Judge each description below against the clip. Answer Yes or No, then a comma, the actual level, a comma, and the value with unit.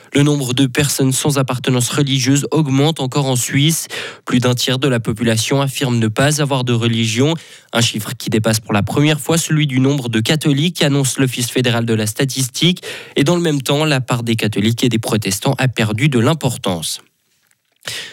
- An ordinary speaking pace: Yes, average, 190 wpm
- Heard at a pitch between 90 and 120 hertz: No, low, 135 Hz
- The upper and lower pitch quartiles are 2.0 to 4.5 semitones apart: Yes, average, 3.6 semitones